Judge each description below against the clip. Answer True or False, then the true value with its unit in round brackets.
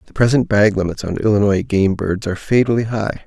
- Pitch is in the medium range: False (105 Hz)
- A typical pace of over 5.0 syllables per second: True (5.9 syllables/s)